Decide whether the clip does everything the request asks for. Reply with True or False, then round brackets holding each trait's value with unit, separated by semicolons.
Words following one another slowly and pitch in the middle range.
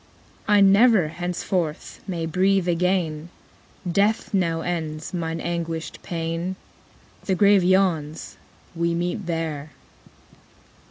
True (100 wpm; 175 Hz)